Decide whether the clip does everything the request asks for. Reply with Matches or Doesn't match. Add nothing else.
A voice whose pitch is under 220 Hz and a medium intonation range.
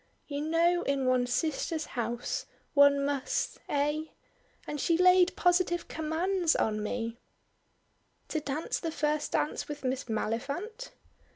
Doesn't match